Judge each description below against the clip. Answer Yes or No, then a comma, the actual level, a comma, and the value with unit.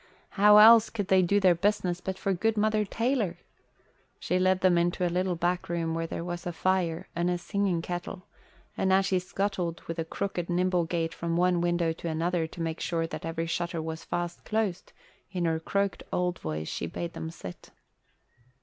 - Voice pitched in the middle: Yes, medium, 175 Hz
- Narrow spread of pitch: Yes, narrow, 2.2 semitones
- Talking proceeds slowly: No, average, 195 wpm